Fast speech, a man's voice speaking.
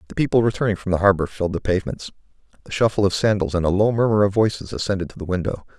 Yes: fast, 240 wpm; male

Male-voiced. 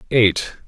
Yes: male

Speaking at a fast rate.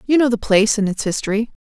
Yes: fast, 260 wpm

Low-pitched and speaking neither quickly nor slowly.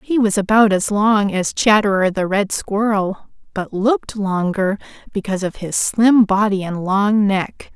No: high, 205 Hz; average, 165 wpm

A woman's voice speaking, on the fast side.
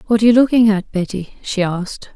Yes: female; fast, 220 wpm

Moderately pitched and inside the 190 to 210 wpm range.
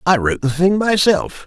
Yes: medium, 170 Hz; fast, 205 wpm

